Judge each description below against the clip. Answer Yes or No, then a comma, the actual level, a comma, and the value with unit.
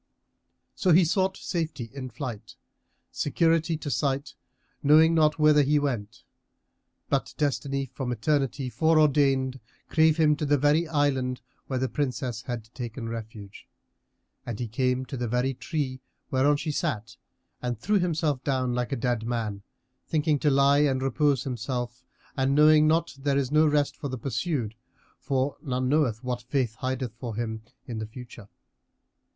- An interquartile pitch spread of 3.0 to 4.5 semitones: Yes, average, 3.5 semitones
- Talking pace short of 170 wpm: Yes, average, 155 wpm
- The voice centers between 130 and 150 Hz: Yes, low, 135 Hz